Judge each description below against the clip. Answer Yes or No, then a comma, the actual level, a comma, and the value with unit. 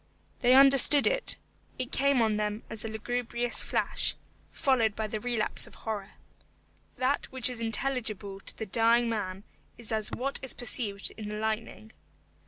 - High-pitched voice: Yes, high, 225 Hz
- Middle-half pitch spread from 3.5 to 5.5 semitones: No, average, 2.8 semitones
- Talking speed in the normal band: Yes, average, 160 wpm